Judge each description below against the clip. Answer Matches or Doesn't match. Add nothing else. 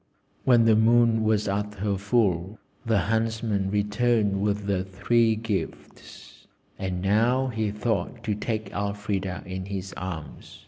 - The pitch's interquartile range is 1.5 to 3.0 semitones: Matches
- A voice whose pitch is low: Matches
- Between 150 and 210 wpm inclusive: Doesn't match